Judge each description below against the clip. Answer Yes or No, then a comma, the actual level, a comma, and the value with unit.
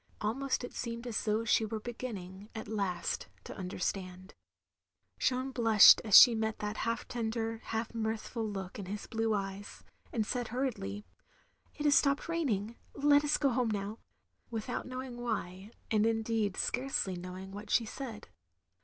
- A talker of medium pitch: No, high, 220 Hz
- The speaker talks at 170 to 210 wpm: No, average, 155 wpm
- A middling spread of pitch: Yes, average, 3.1 semitones